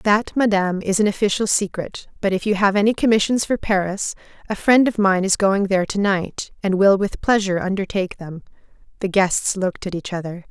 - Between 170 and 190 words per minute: No, average, 200 wpm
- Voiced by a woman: Yes, female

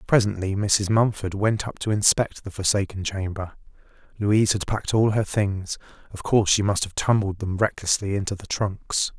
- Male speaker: Yes, male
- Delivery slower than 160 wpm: No, average, 175 wpm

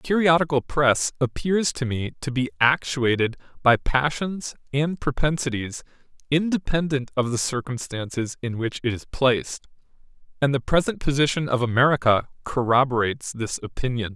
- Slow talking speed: Yes, slow, 130 wpm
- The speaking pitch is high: No, low, 135 Hz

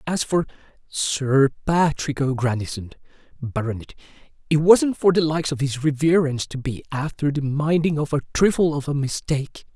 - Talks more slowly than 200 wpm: Yes, average, 155 wpm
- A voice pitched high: No, medium, 145 Hz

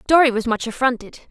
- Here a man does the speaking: No, female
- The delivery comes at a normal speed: Yes, average, 185 wpm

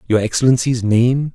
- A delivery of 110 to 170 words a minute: Yes, slow, 135 wpm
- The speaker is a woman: No, male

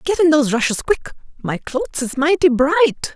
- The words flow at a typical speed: Yes, average, 170 wpm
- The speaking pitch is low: No, very high, 295 Hz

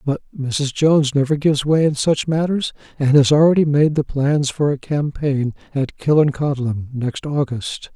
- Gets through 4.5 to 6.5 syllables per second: Yes, 4.6 syllables/s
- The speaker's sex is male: Yes, male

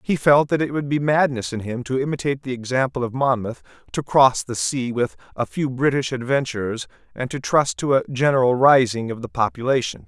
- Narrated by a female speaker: No, male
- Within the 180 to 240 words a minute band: Yes, fast, 205 wpm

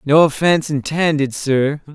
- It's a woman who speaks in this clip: No, male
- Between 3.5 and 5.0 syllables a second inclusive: Yes, 4.6 syllables/s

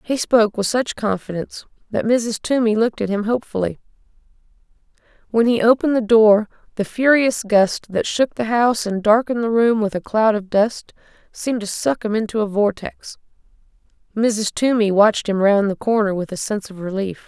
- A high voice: Yes, high, 215 Hz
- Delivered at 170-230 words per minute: Yes, average, 180 wpm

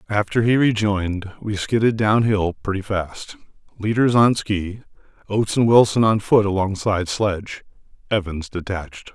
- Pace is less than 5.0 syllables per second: Yes, 4.8 syllables/s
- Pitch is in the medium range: No, low, 105 Hz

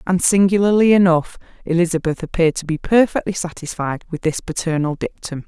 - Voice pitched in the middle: Yes, medium, 175 Hz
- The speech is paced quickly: No, average, 145 wpm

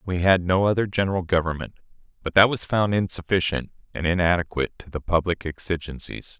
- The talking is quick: No, average, 160 wpm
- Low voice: Yes, very low, 90 Hz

